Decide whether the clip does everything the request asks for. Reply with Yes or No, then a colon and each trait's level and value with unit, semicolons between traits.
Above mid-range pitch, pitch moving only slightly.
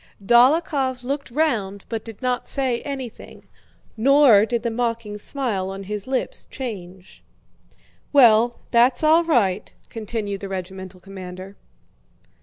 No: high, 230 Hz; average, 4.7 semitones